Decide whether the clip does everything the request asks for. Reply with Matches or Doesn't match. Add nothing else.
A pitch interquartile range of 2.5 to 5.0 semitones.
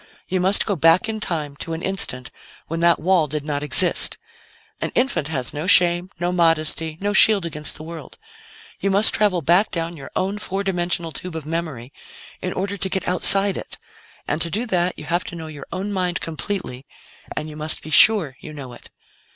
Matches